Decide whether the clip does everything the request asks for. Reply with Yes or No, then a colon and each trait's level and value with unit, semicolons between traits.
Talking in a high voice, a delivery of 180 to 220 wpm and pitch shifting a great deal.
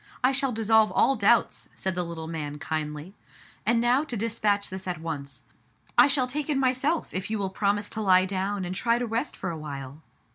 Yes: high, 200 Hz; fast, 205 wpm; wide, 6.0 semitones